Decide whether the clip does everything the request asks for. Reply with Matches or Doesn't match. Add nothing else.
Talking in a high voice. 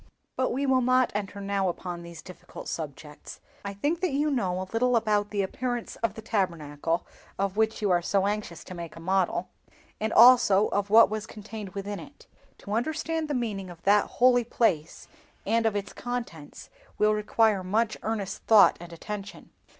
Matches